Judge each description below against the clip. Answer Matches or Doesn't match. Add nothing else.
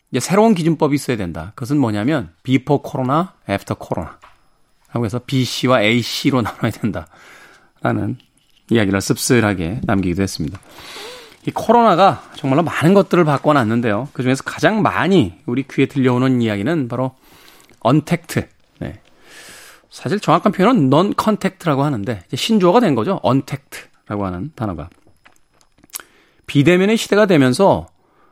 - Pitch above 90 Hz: Matches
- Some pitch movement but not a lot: Doesn't match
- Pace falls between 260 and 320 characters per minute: Doesn't match